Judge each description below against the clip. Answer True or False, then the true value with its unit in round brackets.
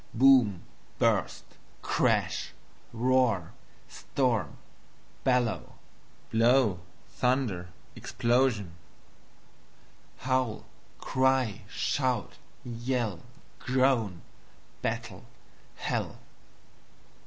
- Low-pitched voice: True (120 Hz)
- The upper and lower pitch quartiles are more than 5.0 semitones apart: False (3.2 semitones)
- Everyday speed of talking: False (55 wpm)